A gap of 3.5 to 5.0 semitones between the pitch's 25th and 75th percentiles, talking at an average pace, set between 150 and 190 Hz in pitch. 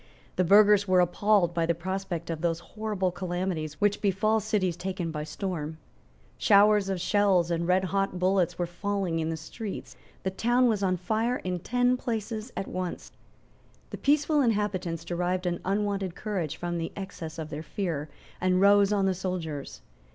No: average, 3.1 semitones; average, 165 wpm; medium, 185 Hz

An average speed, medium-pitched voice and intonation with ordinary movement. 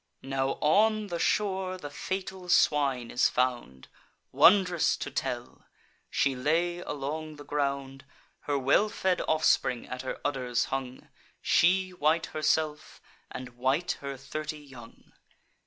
No: slow, 125 wpm; medium, 145 Hz; average, 4.7 semitones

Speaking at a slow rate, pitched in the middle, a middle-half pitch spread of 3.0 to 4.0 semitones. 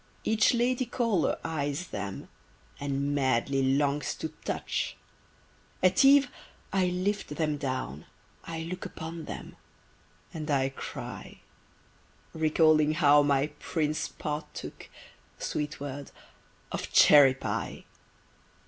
Yes: slow, 105 wpm; medium, 150 Hz; average, 3.3 semitones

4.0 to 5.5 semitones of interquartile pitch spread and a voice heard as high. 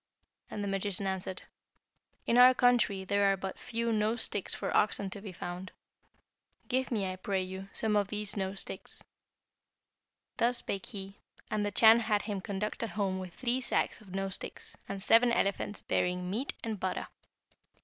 No: average, 2.7 semitones; high, 200 Hz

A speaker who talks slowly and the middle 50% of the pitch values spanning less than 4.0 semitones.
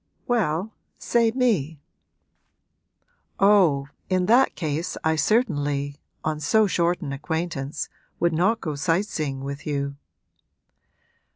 No: slow, 110 wpm; wide, 5.6 semitones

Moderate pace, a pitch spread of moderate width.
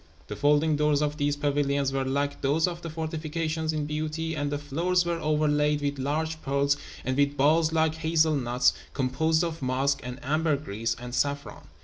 No: average, 175 wpm; narrow, 2.1 semitones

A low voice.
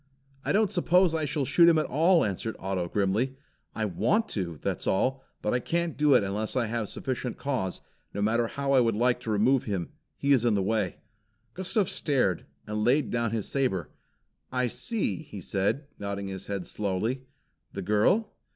Yes: low, 120 Hz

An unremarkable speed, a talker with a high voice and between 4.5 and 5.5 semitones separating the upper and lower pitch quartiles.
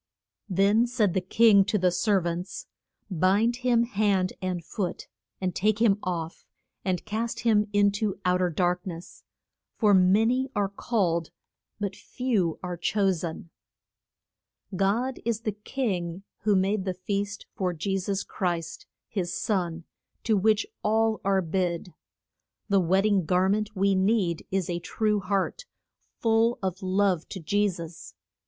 No: average, 150 wpm; high, 195 Hz; average, 2.8 semitones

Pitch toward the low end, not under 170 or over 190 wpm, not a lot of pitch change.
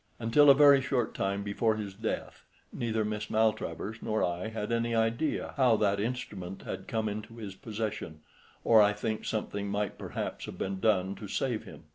Yes: low, 110 Hz; average, 180 wpm; narrow, 2.1 semitones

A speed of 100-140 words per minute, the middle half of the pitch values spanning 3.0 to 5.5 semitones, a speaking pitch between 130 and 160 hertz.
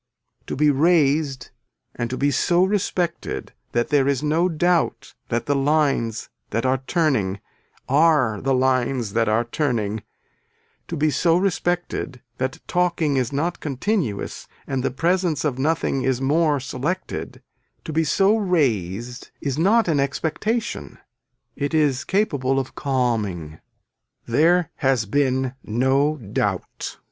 Yes: slow, 135 wpm; average, 4.5 semitones; medium, 140 Hz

